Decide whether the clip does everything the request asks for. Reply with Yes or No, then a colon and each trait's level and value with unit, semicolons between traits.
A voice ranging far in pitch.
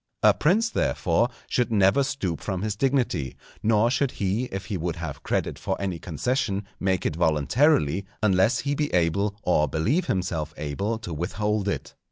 Yes: wide, 6.0 semitones